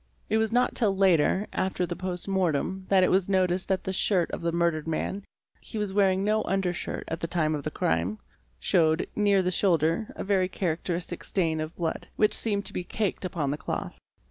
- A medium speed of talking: No, fast, 210 wpm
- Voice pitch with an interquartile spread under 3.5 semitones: Yes, average, 2.9 semitones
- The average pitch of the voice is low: No, medium, 185 Hz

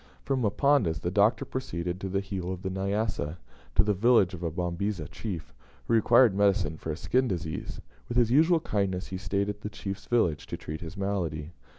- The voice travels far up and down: No, average, 3.8 semitones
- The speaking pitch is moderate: No, very low, 95 Hz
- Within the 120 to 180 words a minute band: No, average, 200 wpm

